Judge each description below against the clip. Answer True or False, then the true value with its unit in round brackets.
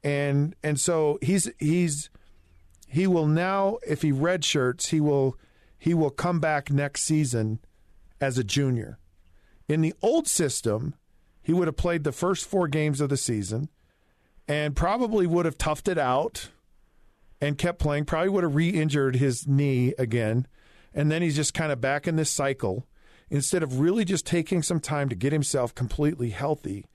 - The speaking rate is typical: True (170 wpm)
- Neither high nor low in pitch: True (145 Hz)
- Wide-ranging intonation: False (4.5 semitones)